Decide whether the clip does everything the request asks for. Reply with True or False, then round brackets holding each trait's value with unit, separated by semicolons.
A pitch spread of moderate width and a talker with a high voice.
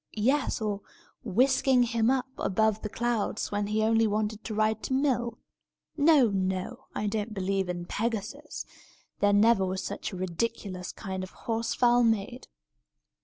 True (3.0 semitones; 220 Hz)